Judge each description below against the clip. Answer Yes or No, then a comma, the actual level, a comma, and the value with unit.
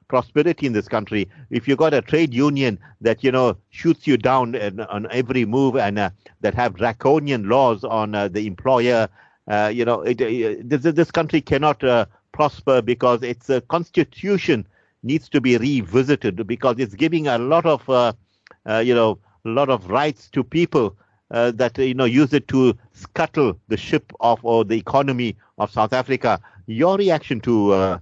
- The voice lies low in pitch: Yes, low, 125 Hz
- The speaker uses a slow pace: No, average, 180 wpm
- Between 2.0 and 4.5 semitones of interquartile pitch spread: Yes, average, 3.9 semitones